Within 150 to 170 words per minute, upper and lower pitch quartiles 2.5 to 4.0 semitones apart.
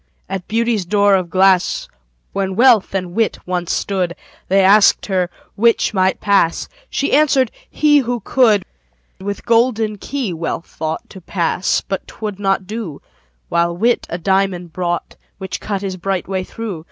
Yes: average, 155 wpm; average, 3.3 semitones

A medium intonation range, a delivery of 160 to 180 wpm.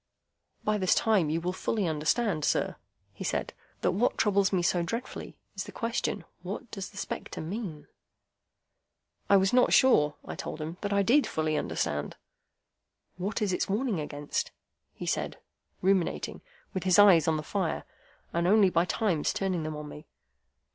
Yes: average, 4.6 semitones; average, 170 wpm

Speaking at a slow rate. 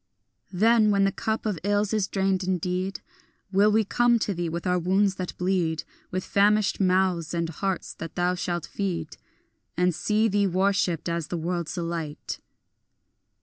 No: average, 160 wpm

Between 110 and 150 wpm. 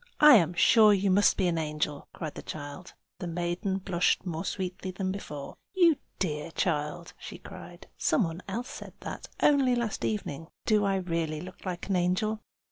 No: average, 185 wpm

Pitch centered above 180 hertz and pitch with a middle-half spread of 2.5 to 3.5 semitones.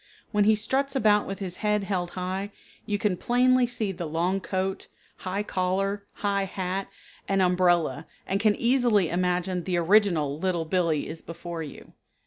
Yes: high, 190 Hz; average, 2.8 semitones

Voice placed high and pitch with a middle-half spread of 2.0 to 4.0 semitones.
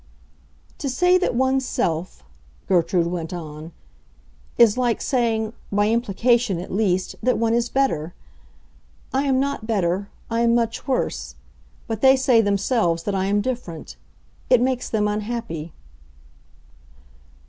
No: high, 225 Hz; average, 5.1 semitones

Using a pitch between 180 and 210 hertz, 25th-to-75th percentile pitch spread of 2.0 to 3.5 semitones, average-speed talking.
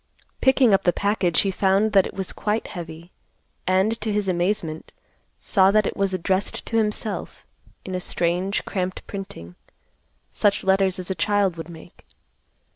Yes: high, 190 Hz; narrow, 2.4 semitones; average, 160 wpm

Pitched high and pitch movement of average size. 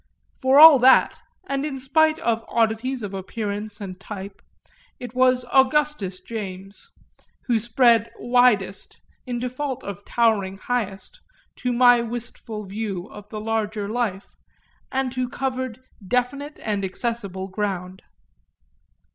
Yes: high, 230 Hz; average, 4.0 semitones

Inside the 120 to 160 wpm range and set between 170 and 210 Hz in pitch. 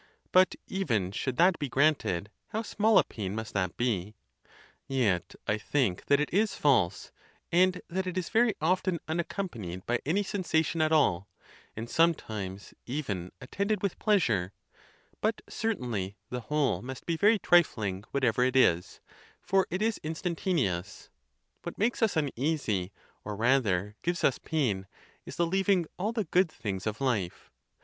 No: average, 155 wpm; medium, 140 Hz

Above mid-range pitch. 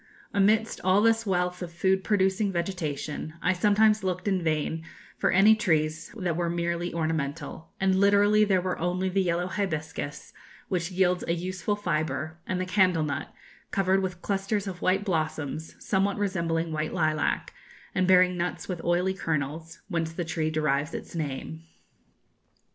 No: medium, 180 Hz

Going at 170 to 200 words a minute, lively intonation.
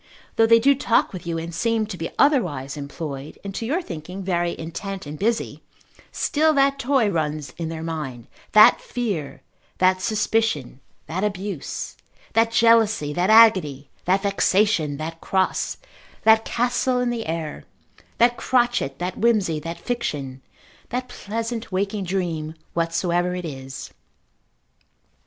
No: average, 140 wpm; wide, 6.1 semitones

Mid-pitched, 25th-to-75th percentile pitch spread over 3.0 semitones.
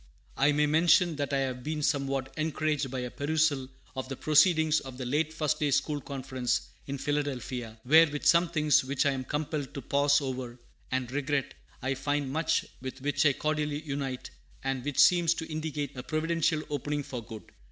No: medium, 145 Hz; average, 2.7 semitones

